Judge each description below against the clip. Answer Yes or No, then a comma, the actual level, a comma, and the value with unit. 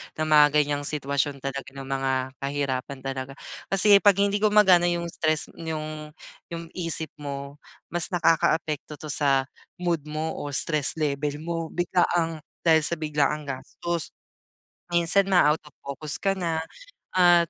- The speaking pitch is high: No, medium, 155 Hz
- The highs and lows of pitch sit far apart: No, average, 3.3 semitones